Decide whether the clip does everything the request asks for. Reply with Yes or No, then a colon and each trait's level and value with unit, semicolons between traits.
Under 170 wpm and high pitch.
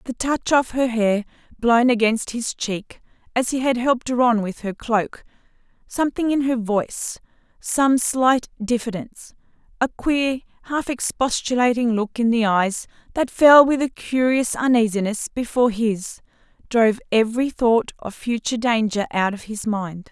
Yes: average, 150 wpm; high, 235 Hz